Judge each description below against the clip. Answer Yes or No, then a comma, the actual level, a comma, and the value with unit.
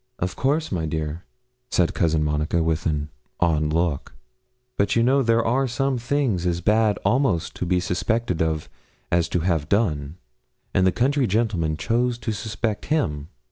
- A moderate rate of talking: Yes, average, 165 wpm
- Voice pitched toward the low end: Yes, very low, 90 Hz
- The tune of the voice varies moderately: No, wide, 6.5 semitones